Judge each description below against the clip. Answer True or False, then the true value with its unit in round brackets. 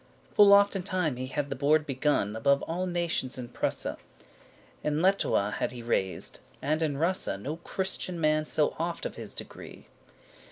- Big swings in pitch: False (5.0 semitones)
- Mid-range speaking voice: True (155 Hz)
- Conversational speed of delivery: True (170 wpm)